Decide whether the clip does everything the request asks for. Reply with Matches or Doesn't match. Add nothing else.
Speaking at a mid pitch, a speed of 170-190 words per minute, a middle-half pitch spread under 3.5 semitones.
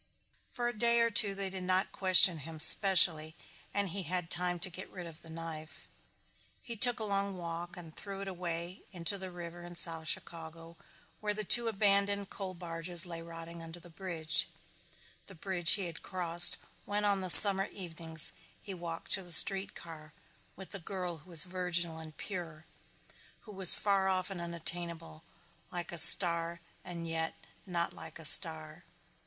Matches